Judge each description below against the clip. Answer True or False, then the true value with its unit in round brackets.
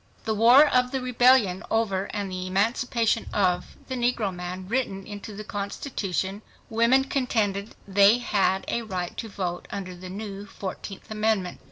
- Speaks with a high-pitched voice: True (205 Hz)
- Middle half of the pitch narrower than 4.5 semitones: True (3.5 semitones)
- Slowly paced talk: False (155 wpm)